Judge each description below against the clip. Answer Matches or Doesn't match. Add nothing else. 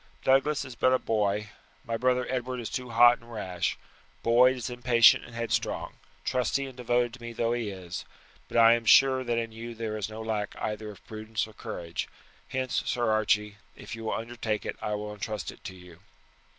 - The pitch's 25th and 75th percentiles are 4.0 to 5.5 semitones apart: Doesn't match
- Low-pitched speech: Matches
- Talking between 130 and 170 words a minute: Doesn't match